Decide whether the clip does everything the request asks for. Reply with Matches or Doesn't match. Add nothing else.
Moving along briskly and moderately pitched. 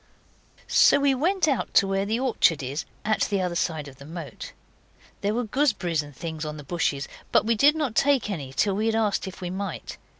Doesn't match